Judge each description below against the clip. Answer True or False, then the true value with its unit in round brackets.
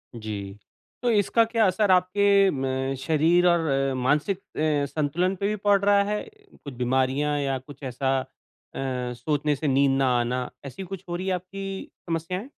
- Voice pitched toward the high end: False (150 Hz)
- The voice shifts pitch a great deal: True (6.3 semitones)